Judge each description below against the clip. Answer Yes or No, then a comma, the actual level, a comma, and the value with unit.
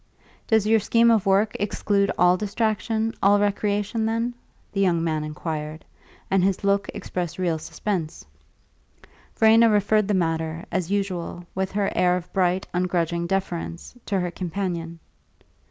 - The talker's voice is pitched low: No, high, 190 Hz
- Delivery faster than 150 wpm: No, average, 140 wpm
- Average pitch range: Yes, average, 3.1 semitones